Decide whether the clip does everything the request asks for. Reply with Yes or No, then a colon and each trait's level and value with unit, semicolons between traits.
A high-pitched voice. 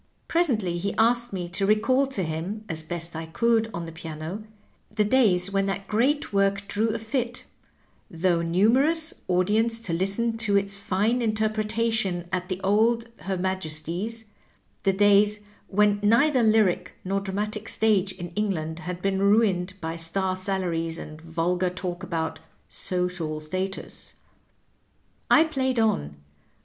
Yes: high, 195 Hz